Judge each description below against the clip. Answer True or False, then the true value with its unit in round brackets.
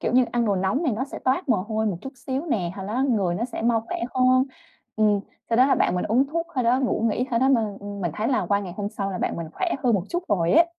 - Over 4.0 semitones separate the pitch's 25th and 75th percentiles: True (4.4 semitones)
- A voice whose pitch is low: False (230 Hz)